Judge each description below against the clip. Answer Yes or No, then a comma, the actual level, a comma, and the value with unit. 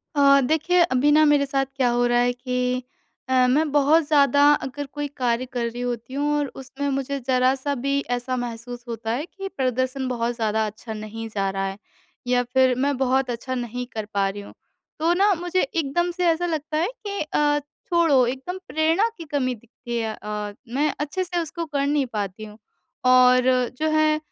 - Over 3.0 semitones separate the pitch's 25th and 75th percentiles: Yes, average, 3.5 semitones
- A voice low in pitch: No, very high, 260 Hz